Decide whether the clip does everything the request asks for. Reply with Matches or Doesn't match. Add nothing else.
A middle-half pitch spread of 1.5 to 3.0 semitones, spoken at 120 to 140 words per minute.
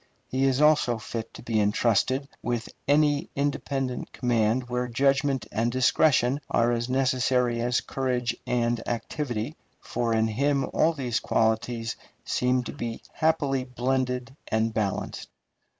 Matches